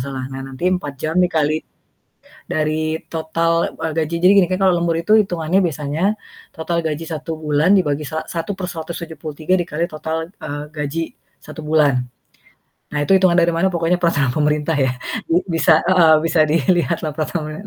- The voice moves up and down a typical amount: No, narrow, 2.2 semitones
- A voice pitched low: No, medium, 160 Hz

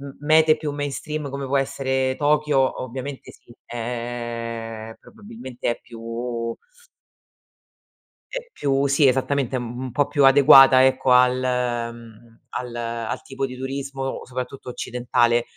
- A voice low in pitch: Yes, low, 130 Hz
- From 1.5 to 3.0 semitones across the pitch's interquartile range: Yes, narrow, 2.6 semitones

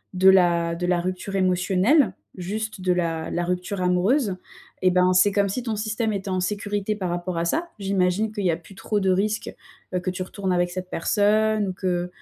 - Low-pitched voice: No, medium, 185 Hz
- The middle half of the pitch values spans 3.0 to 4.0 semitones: No, narrow, 2.4 semitones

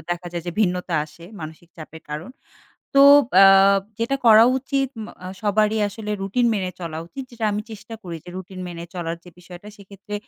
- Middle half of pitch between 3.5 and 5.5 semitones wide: Yes, average, 3.9 semitones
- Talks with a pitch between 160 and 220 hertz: Yes, high, 190 Hz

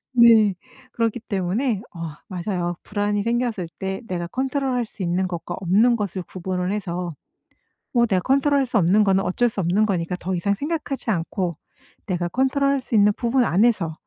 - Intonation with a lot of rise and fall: No, average, 4.8 semitones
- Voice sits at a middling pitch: No, high, 200 Hz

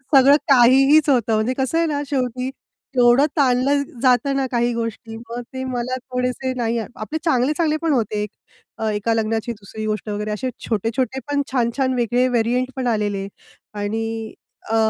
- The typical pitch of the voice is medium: No, high, 245 Hz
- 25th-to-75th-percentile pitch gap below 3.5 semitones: Yes, average, 2.8 semitones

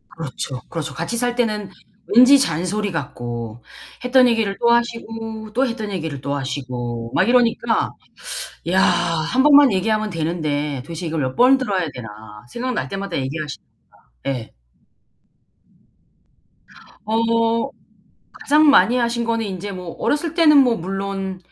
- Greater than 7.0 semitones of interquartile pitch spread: Yes, wide, 7.4 semitones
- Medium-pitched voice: No, high, 195 Hz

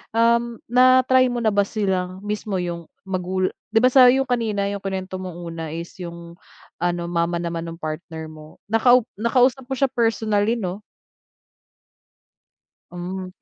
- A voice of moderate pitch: No, high, 200 Hz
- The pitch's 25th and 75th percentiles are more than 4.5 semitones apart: Yes, average, 5.1 semitones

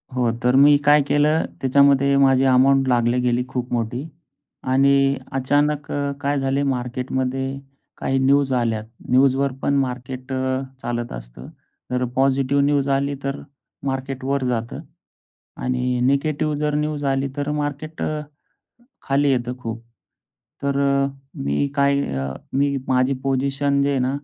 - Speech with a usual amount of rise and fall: No, narrow, 1.9 semitones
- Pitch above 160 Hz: No, low, 135 Hz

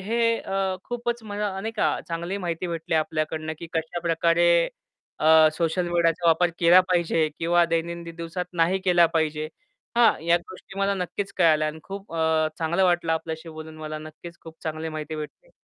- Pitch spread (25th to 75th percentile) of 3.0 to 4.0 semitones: No, narrow, 2.4 semitones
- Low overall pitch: No, medium, 170 Hz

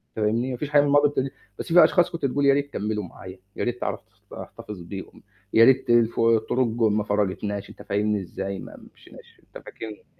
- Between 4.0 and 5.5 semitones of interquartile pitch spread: Yes, average, 4.5 semitones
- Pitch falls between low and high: No, low, 115 Hz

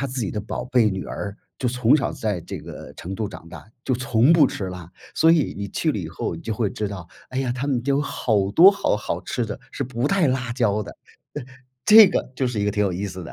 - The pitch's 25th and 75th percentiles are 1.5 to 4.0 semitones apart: No, average, 4.7 semitones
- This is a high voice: No, low, 115 Hz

